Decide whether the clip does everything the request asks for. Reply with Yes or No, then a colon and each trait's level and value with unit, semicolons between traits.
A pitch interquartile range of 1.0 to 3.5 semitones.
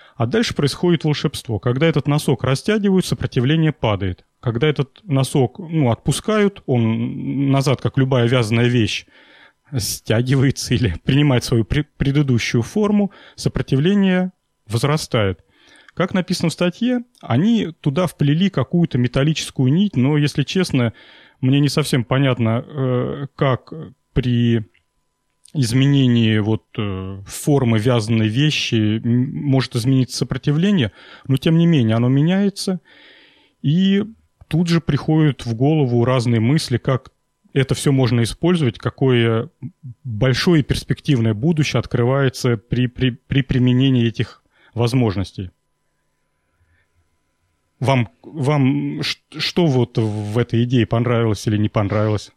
No: average, 4.4 semitones